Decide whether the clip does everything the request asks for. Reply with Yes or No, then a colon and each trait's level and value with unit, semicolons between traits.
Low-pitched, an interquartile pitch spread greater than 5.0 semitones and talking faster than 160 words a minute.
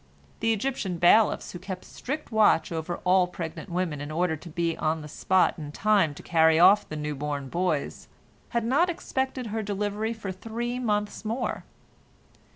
No: medium, 185 Hz; wide, 5.4 semitones; average, 170 wpm